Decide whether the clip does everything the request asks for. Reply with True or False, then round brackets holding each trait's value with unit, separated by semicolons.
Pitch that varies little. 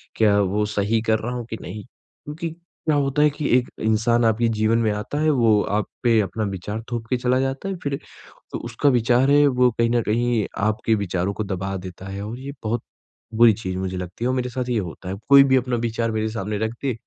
False (3.3 semitones)